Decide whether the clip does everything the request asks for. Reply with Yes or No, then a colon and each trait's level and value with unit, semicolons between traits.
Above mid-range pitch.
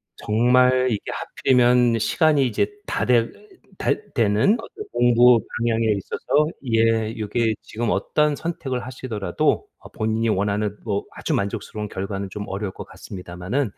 No: low, 115 Hz